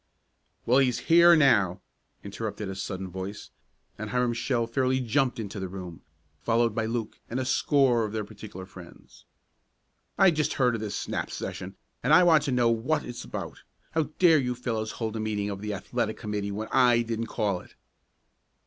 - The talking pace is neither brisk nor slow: Yes, average, 185 wpm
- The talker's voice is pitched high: No, low, 115 Hz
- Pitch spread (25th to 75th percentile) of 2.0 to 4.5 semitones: Yes, average, 3.6 semitones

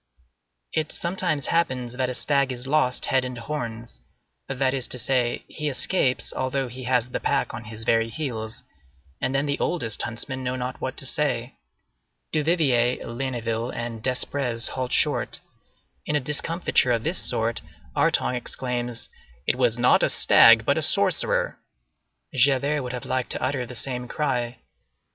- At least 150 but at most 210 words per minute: Yes, average, 160 wpm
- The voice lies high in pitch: No, low, 125 Hz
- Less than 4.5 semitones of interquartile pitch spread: Yes, narrow, 2.4 semitones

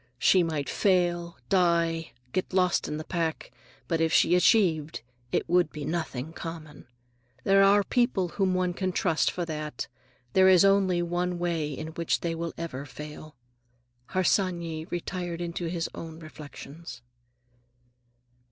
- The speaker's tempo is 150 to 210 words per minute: No, average, 140 wpm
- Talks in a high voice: No, medium, 170 Hz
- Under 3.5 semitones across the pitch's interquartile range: Yes, narrow, 2.4 semitones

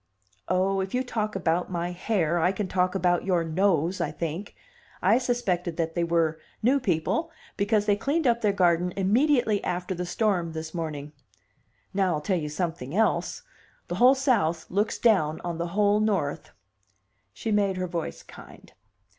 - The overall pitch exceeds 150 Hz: Yes, medium, 185 Hz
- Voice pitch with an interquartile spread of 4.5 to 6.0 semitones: No, average, 3.8 semitones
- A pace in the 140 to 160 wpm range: No, average, 170 wpm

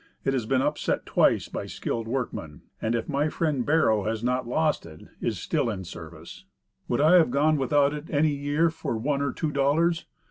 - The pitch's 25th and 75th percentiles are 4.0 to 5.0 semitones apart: Yes, average, 4.7 semitones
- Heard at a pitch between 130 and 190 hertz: Yes, medium, 140 Hz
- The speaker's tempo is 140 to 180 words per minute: No, average, 200 wpm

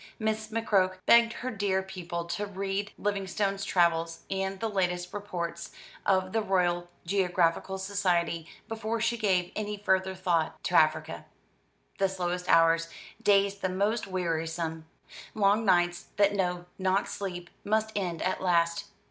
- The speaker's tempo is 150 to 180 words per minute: No, average, 140 wpm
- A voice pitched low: No, high, 190 Hz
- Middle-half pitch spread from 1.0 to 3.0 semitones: Yes, narrow, 2.5 semitones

